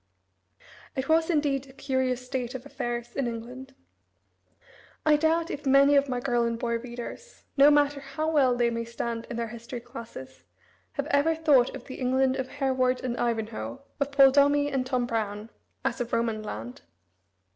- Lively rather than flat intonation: No, average, 2.9 semitones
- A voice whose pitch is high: Yes, very high, 255 Hz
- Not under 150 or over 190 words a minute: Yes, average, 175 wpm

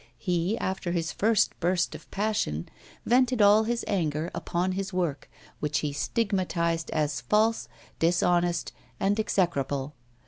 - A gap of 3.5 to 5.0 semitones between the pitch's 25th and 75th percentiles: Yes, average, 4.1 semitones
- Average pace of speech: No, slow, 130 wpm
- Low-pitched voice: No, medium, 180 Hz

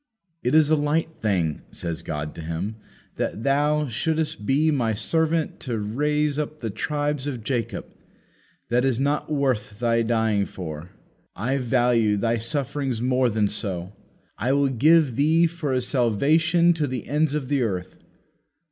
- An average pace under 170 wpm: Yes, average, 155 wpm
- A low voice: Yes, low, 130 Hz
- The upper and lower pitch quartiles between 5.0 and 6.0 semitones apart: Yes, average, 5.3 semitones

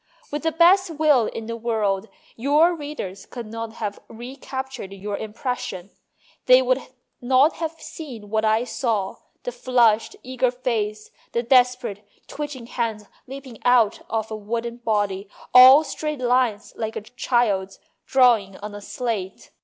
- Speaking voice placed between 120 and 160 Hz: No, high, 235 Hz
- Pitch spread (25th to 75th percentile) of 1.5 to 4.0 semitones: Yes, average, 3.4 semitones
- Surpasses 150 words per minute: No, average, 145 wpm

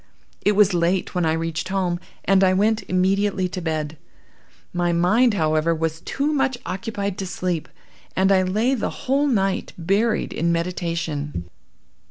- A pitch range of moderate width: Yes, average, 3.4 semitones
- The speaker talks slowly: No, average, 155 wpm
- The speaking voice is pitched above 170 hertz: Yes, medium, 185 Hz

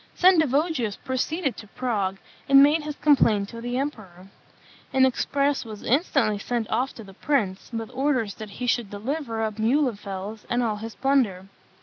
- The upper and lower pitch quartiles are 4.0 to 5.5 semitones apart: Yes, average, 4.7 semitones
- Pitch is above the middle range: Yes, high, 240 Hz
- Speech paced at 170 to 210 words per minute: No, average, 160 wpm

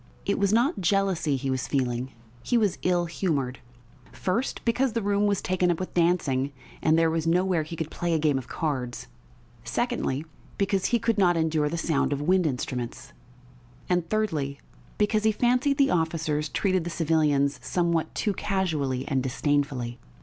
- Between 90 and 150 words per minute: No, average, 170 wpm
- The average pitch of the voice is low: No, medium, 165 Hz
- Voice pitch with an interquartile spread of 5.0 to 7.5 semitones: Yes, average, 5.3 semitones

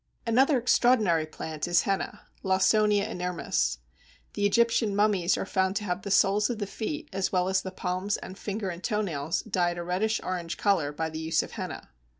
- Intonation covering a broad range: No, average, 3.1 semitones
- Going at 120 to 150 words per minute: No, average, 190 wpm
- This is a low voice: No, high, 190 Hz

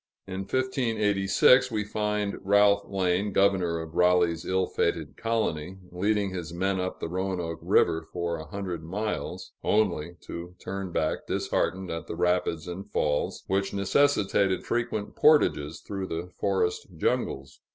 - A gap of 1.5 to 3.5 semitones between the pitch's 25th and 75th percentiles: Yes, average, 3.1 semitones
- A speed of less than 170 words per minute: Yes, average, 140 wpm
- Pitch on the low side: Yes, very low, 95 Hz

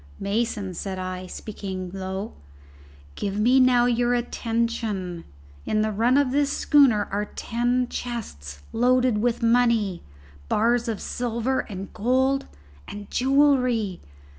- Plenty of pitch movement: No, average, 3.8 semitones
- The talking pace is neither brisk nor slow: No, slow, 120 wpm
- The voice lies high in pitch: Yes, high, 230 Hz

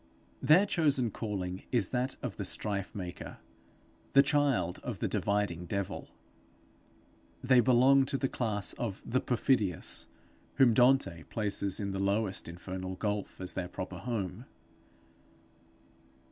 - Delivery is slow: Yes, slow, 130 wpm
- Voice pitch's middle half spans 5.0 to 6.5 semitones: Yes, average, 5.3 semitones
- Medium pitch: No, low, 105 Hz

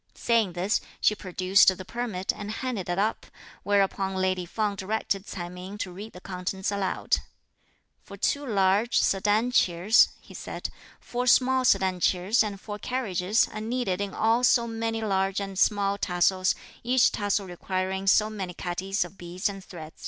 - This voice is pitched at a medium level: No, high, 195 Hz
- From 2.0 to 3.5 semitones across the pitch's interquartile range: Yes, average, 2.7 semitones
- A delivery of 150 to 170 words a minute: Yes, average, 165 wpm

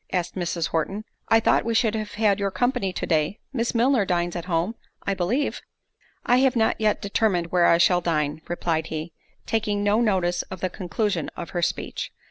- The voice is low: No, high, 190 Hz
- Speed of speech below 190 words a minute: No, average, 195 wpm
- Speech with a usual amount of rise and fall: Yes, average, 4.2 semitones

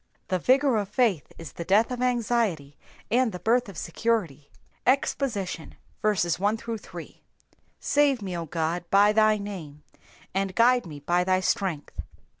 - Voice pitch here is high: Yes, high, 200 Hz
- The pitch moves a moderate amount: No, wide, 5.7 semitones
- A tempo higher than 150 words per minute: No, slow, 135 wpm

